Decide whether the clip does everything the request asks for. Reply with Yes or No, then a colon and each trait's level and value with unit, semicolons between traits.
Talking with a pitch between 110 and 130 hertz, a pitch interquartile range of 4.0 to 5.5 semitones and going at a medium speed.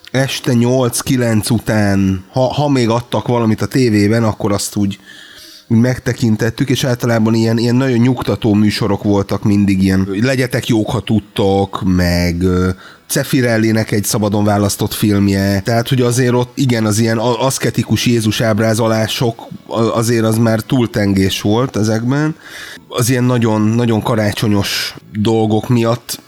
No: low, 115 Hz; average, 2.9 semitones; average, 135 wpm